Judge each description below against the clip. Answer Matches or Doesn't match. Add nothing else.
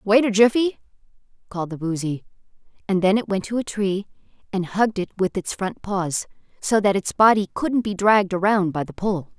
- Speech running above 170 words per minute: Matches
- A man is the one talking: Doesn't match